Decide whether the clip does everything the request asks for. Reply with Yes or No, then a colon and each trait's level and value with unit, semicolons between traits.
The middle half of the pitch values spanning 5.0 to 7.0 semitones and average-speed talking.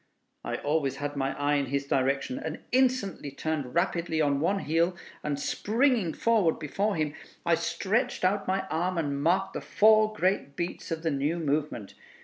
Yes: average, 5.3 semitones; average, 170 wpm